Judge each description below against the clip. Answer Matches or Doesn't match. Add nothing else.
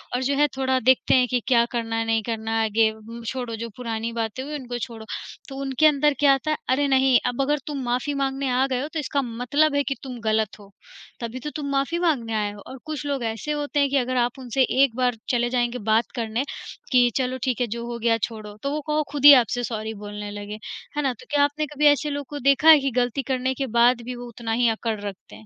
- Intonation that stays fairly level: Doesn't match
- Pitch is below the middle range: Doesn't match